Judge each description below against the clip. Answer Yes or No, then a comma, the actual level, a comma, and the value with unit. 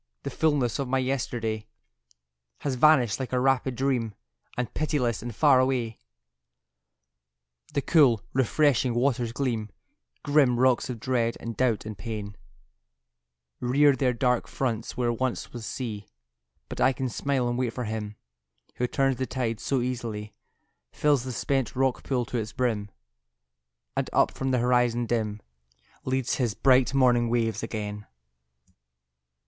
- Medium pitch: No, low, 125 Hz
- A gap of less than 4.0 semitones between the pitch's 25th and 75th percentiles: Yes, narrow, 2.5 semitones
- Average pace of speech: Yes, average, 145 wpm